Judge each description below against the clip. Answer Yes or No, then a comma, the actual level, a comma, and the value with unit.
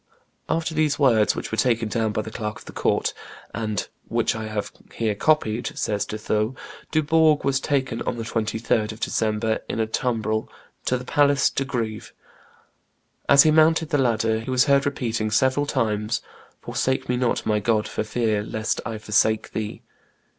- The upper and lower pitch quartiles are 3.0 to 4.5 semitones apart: Yes, average, 3.9 semitones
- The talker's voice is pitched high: No, low, 115 Hz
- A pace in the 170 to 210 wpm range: Yes, average, 175 wpm